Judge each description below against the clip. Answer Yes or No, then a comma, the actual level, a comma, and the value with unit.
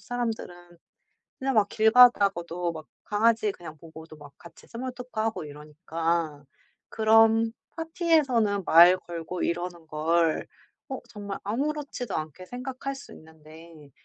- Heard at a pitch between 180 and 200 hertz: Yes, high, 190 Hz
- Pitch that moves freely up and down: Yes, wide, 6.2 semitones